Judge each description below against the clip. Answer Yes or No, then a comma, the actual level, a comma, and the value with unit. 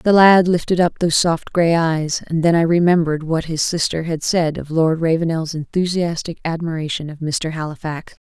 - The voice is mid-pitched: Yes, medium, 165 Hz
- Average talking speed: Yes, average, 180 wpm